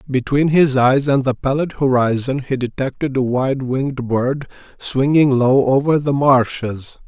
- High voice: No, low, 135 Hz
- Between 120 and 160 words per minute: Yes, average, 155 wpm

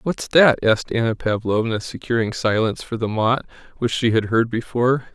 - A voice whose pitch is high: No, low, 115 Hz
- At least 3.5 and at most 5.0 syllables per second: No, 5.4 syllables/s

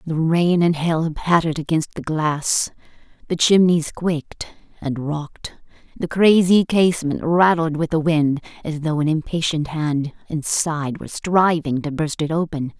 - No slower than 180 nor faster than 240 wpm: No, average, 150 wpm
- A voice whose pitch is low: No, medium, 160 Hz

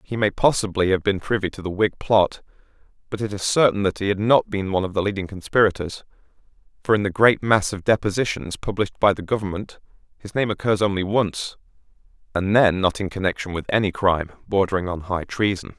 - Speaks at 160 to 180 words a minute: No, average, 200 wpm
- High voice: No, low, 100 Hz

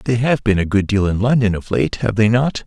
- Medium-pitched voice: No, low, 110 Hz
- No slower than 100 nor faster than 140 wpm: No, fast, 295 wpm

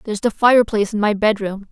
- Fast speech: Yes, fast, 210 wpm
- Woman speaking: Yes, female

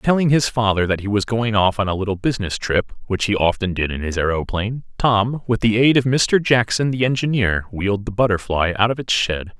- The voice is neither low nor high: No, low, 110 Hz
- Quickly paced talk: Yes, fast, 225 wpm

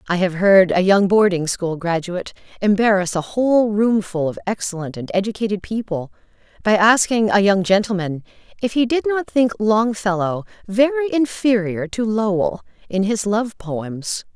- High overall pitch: Yes, high, 200 Hz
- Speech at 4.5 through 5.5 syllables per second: Yes, 4.7 syllables/s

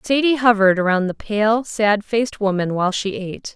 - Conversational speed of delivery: Yes, average, 185 wpm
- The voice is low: No, high, 210 Hz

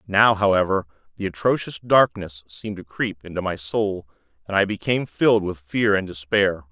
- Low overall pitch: Yes, very low, 95 Hz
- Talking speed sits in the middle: Yes, average, 170 wpm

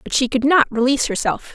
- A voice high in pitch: Yes, very high, 255 Hz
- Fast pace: Yes, fast, 235 wpm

